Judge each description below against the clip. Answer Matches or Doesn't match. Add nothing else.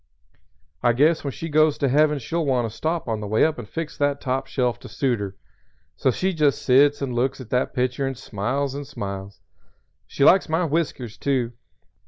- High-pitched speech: Doesn't match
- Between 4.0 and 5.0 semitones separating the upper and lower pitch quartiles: Doesn't match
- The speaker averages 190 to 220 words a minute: Matches